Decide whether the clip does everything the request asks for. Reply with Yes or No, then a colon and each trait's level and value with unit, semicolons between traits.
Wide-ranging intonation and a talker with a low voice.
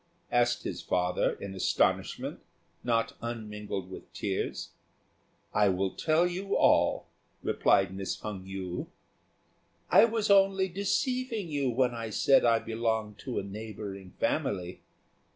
Yes: wide, 8.2 semitones; low, 115 Hz